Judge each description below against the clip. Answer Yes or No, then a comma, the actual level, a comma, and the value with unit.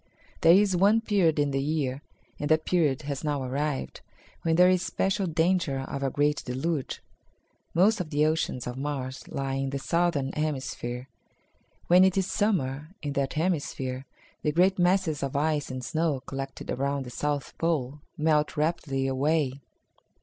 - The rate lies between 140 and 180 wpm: Yes, average, 165 wpm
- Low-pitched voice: No, medium, 150 Hz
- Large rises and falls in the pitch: No, average, 3.8 semitones